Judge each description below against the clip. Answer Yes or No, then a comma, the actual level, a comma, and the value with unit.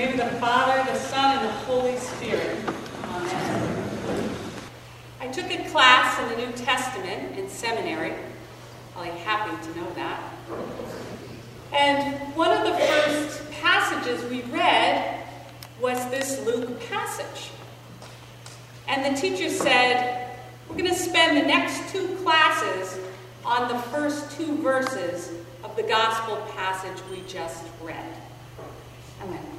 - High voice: Yes, very high, 260 Hz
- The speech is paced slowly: Yes, slow, 125 wpm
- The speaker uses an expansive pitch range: No, average, 4.6 semitones